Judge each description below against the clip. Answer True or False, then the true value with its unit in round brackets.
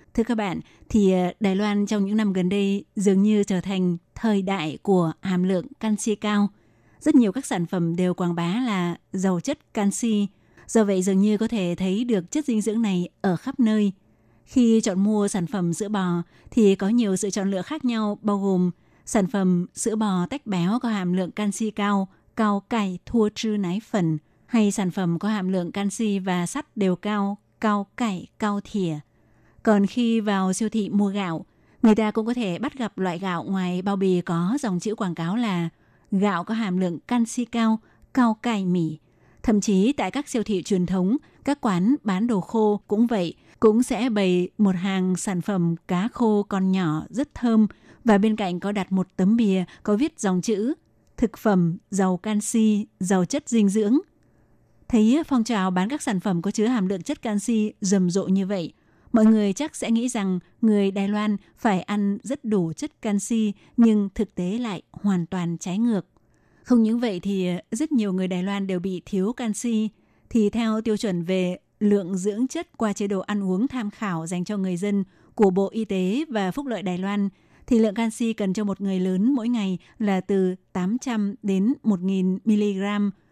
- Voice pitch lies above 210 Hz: False (205 Hz)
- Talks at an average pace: True (200 wpm)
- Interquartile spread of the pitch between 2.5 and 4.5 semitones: True (3.0 semitones)